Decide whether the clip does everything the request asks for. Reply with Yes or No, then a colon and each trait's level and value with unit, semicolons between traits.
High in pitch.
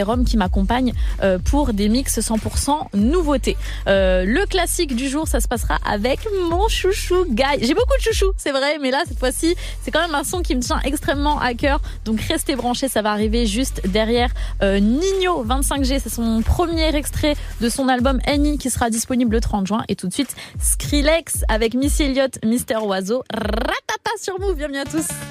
Yes: very high, 270 Hz